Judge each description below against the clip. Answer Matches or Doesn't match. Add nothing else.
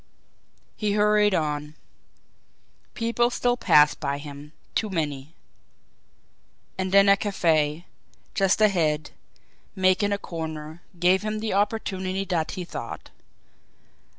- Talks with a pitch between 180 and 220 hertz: Matches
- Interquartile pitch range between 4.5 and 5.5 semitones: Matches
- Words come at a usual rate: Doesn't match